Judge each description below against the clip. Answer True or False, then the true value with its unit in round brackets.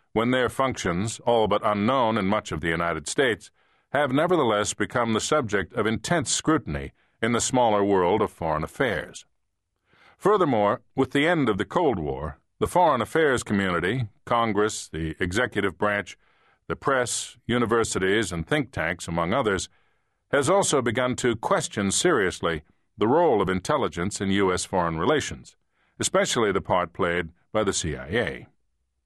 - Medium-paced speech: True (150 wpm)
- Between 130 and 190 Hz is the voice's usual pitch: False (105 Hz)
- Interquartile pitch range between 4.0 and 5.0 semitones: True (4.4 semitones)